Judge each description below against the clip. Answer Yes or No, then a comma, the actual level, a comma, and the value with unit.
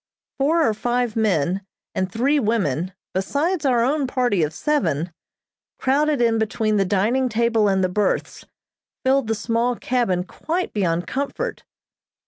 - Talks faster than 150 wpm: No, average, 140 wpm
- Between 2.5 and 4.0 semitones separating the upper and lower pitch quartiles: No, wide, 5.5 semitones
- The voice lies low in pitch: No, high, 230 Hz